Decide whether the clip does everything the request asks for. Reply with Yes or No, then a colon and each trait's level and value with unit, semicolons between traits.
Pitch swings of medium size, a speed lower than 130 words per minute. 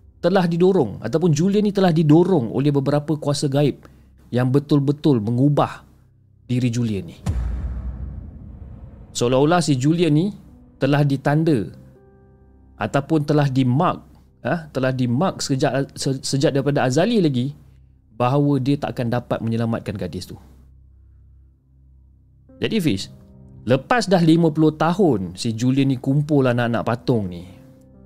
No: wide, 8.5 semitones; average, 120 wpm